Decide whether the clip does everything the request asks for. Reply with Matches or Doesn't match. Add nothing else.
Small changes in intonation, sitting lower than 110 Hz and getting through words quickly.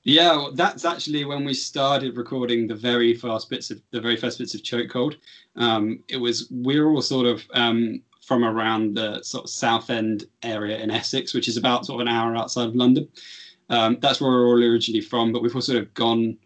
Doesn't match